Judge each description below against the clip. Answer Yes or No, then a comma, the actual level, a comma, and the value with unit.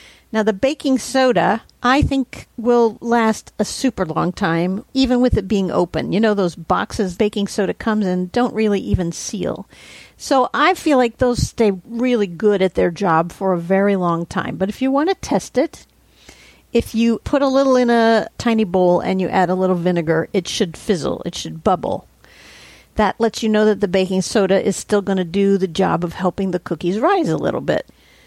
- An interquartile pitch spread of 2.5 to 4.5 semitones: Yes, average, 4.0 semitones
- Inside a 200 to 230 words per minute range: Yes, fast, 205 wpm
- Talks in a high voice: Yes, high, 205 Hz